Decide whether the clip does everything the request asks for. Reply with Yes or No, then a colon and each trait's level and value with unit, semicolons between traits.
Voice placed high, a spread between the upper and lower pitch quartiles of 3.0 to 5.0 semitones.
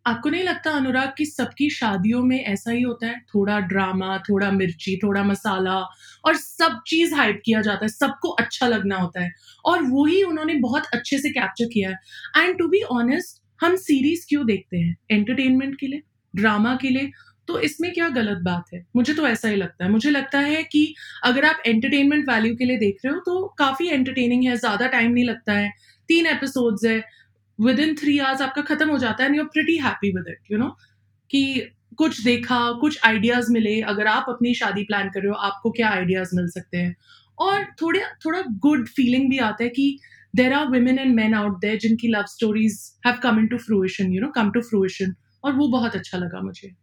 No: high, 240 Hz; wide, 5.5 semitones